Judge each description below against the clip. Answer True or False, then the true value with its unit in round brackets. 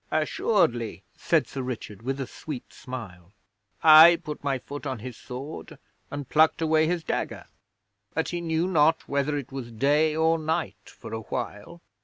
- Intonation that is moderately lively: True (3.9 semitones)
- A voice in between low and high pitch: True (145 Hz)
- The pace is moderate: True (160 wpm)